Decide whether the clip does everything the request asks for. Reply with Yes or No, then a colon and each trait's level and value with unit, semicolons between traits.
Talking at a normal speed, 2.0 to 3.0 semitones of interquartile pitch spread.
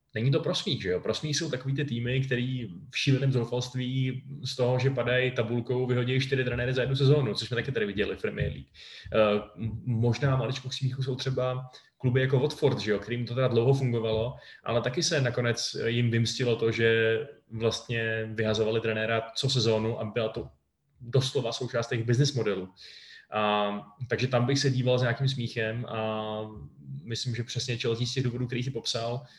No: fast, 180 wpm; narrow, 2.4 semitones